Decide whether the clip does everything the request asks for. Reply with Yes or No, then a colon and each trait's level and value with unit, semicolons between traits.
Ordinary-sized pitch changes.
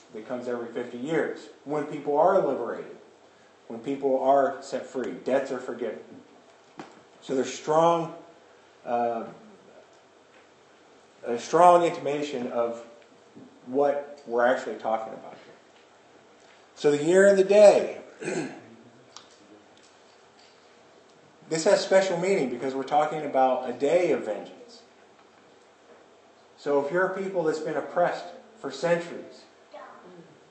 Yes: average, 5.0 semitones